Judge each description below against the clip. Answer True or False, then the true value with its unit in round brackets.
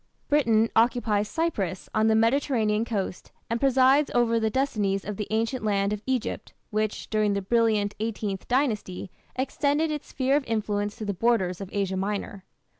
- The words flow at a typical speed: True (165 wpm)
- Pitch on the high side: True (220 Hz)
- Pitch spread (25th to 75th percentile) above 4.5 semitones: False (3.7 semitones)